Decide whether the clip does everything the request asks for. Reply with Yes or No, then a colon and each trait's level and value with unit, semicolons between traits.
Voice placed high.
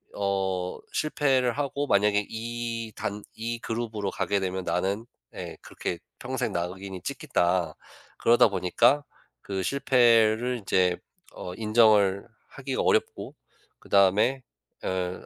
No: low, 105 Hz